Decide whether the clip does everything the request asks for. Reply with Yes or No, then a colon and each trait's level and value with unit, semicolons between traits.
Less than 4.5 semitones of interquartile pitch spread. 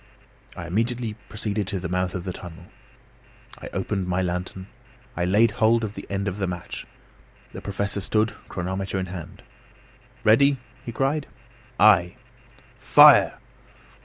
Yes: average, 3.3 semitones